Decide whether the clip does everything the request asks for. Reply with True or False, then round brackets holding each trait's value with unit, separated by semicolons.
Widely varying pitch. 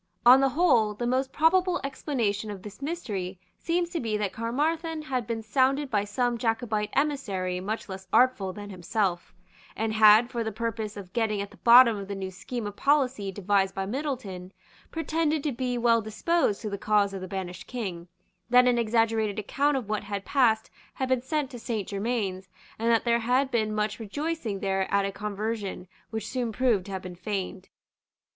False (4.2 semitones)